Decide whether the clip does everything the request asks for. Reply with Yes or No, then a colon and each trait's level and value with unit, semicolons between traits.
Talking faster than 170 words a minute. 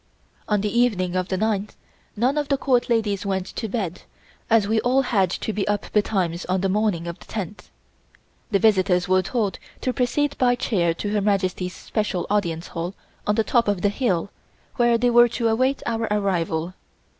Yes: average, 190 wpm